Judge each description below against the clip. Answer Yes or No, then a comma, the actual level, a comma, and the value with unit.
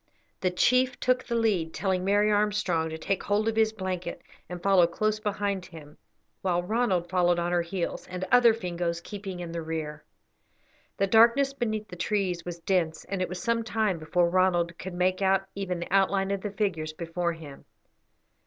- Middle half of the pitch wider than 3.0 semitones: Yes, average, 3.4 semitones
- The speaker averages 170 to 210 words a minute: Yes, average, 185 wpm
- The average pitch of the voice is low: No, medium, 185 Hz